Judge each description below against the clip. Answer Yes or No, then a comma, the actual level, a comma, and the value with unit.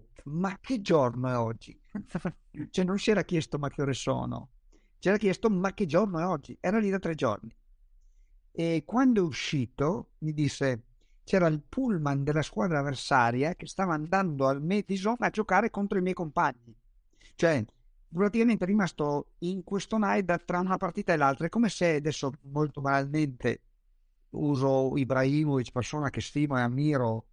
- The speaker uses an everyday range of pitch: No, wide, 5.8 semitones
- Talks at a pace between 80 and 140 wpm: No, average, 165 wpm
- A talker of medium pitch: Yes, medium, 155 Hz